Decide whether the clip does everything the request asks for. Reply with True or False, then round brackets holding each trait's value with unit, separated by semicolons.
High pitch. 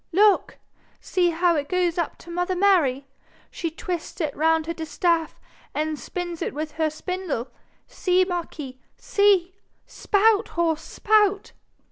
True (345 Hz)